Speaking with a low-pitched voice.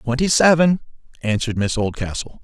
Yes: low, 130 Hz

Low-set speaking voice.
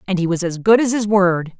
No: high, 190 Hz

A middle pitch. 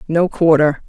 Yes: medium, 160 Hz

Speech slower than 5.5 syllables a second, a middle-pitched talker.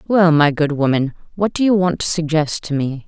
Yes: 5.2 syllables/s; medium, 160 Hz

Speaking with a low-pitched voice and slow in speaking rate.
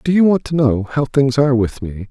No: low, 130 Hz; fast, 255 wpm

